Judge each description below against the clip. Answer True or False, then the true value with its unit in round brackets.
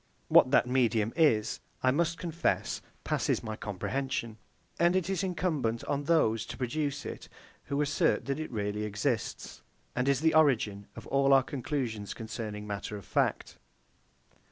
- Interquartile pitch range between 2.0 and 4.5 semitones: False (5.6 semitones)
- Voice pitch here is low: True (130 Hz)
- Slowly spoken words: False (155 wpm)